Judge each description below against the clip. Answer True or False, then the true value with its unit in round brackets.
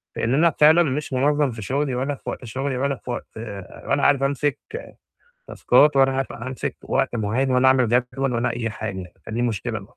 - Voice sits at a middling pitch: False (130 Hz)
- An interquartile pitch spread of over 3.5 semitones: False (2.8 semitones)